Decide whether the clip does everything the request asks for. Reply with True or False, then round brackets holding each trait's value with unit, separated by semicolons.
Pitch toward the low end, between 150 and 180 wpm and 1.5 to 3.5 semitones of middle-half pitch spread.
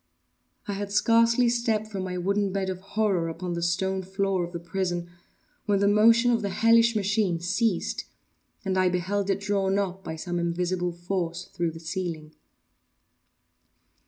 False (190 Hz; 160 wpm; 2.7 semitones)